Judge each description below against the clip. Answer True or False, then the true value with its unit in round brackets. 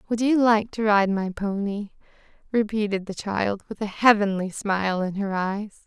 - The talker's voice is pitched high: True (205 Hz)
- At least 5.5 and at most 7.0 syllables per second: False (4.6 syllables/s)